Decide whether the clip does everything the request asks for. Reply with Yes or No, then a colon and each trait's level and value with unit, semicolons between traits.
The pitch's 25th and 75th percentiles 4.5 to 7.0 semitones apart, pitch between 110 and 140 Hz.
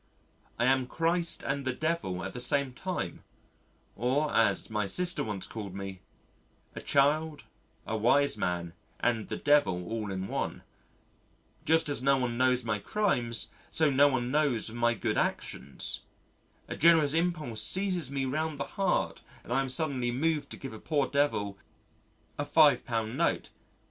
Yes: average, 5.2 semitones; low, 135 Hz